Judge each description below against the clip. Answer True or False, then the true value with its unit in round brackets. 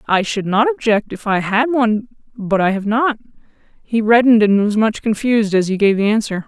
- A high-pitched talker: True (215 Hz)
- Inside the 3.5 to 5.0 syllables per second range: False (5.5 syllables/s)